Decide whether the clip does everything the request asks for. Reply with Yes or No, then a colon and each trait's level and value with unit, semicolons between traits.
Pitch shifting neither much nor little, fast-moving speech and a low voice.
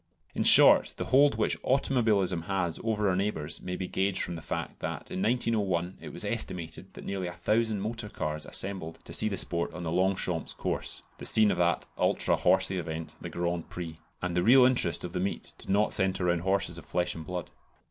Yes: average, 3.3 semitones; fast, 210 wpm; very low, 95 Hz